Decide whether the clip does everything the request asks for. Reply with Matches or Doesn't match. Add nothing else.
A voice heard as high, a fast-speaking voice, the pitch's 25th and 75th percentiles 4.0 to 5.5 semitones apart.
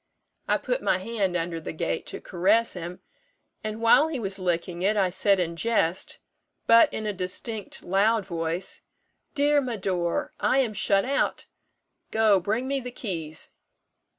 Doesn't match